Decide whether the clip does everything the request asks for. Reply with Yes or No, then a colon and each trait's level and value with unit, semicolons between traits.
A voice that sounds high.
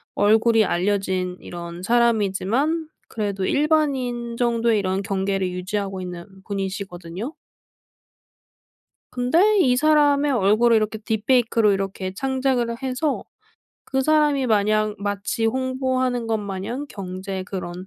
Yes: high, 220 Hz